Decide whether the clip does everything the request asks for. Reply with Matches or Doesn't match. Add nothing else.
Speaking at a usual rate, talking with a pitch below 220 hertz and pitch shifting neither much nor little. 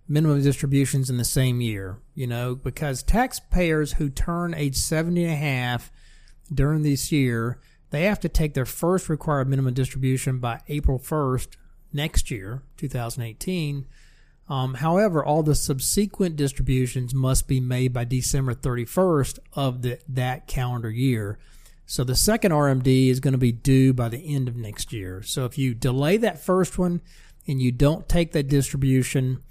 Matches